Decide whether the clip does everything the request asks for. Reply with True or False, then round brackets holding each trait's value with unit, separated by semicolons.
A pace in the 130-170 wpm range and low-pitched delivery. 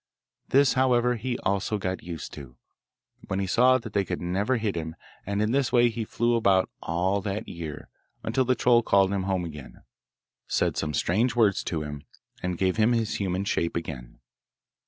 False (185 wpm; 100 Hz)